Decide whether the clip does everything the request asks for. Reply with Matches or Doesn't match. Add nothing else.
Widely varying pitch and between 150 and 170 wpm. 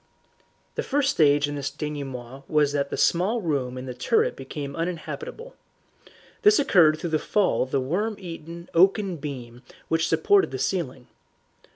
Matches